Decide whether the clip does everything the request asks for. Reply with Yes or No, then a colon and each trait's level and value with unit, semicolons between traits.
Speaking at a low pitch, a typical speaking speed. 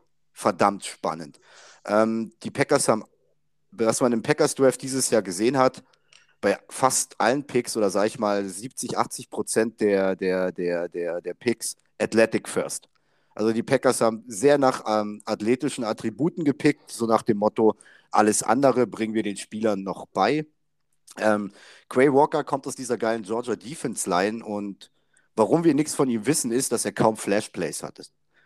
Yes: low, 115 Hz; average, 170 wpm